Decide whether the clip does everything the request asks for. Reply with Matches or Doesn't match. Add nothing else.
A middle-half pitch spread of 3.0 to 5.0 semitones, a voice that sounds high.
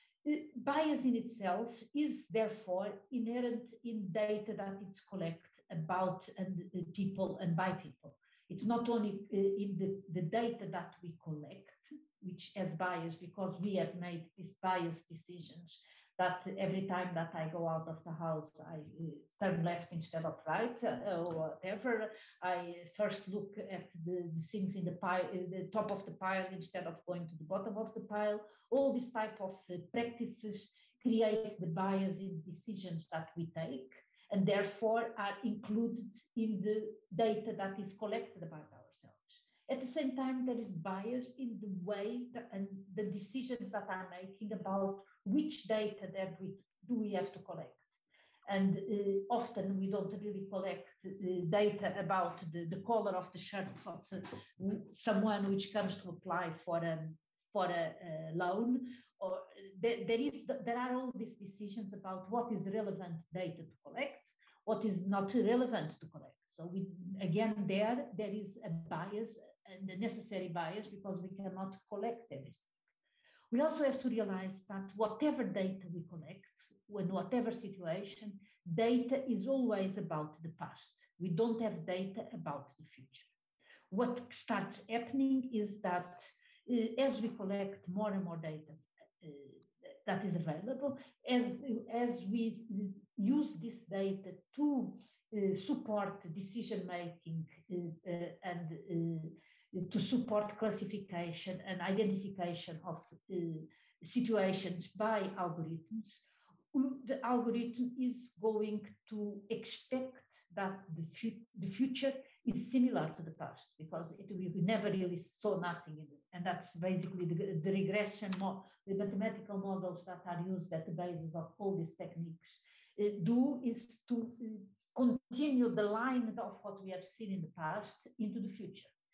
Matches